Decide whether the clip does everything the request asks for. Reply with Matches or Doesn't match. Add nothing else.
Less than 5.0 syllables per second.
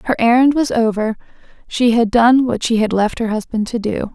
Doesn't match